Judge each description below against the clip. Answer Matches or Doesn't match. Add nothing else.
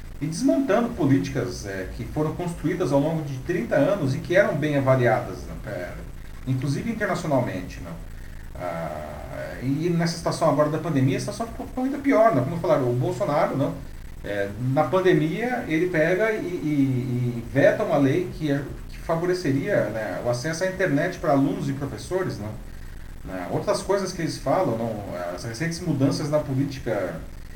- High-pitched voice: Doesn't match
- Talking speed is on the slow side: Doesn't match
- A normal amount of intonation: Doesn't match